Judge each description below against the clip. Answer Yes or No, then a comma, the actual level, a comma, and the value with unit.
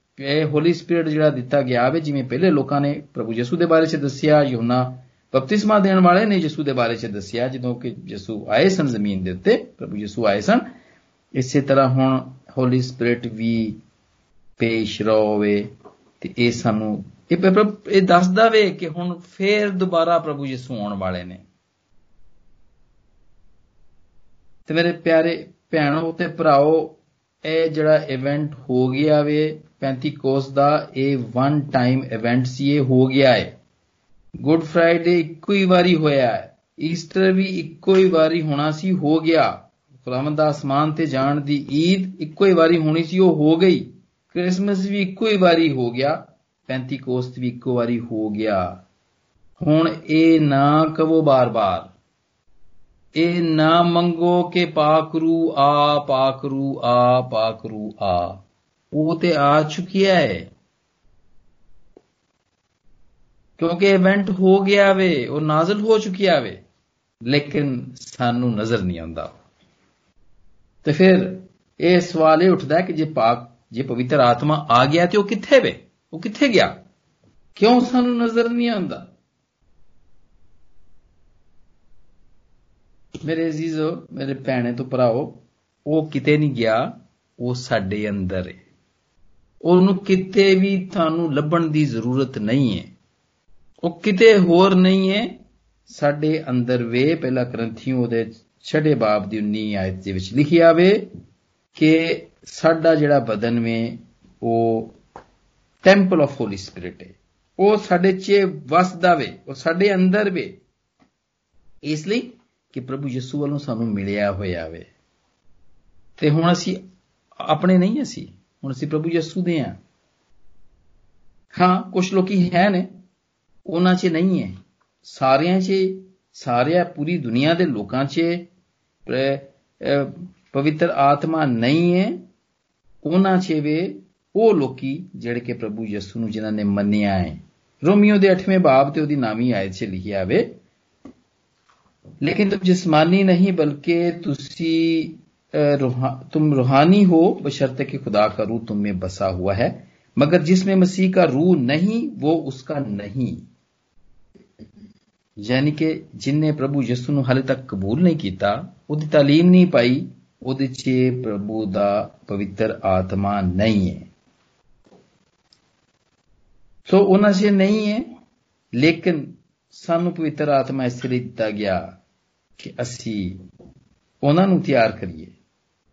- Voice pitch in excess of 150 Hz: No, medium, 145 Hz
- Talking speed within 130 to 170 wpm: Yes, average, 135 wpm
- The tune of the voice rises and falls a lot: Yes, wide, 6.6 semitones